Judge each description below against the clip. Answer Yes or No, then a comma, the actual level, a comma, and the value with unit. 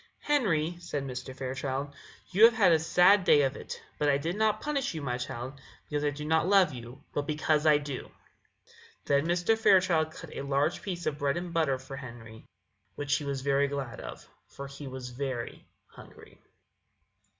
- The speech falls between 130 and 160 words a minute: No, average, 185 wpm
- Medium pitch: Yes, medium, 145 Hz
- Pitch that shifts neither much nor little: Yes, average, 4.1 semitones